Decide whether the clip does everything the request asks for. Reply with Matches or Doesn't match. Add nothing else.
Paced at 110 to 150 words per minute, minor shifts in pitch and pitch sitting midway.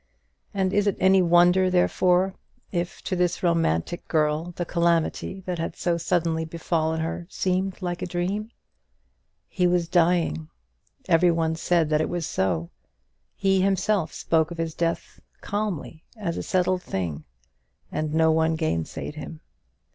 Matches